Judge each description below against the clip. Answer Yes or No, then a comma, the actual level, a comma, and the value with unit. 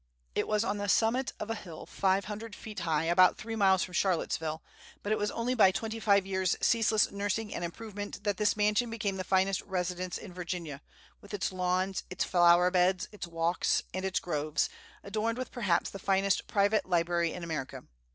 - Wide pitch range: No, average, 3.0 semitones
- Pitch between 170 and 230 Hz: Yes, high, 190 Hz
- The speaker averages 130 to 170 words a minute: No, average, 190 wpm